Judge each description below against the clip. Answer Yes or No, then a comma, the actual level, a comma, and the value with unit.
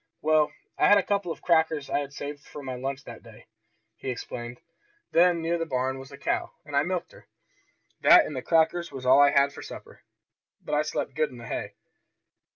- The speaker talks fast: Yes, fast, 215 wpm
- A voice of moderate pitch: Yes, medium, 145 Hz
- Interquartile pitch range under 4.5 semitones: Yes, average, 3.5 semitones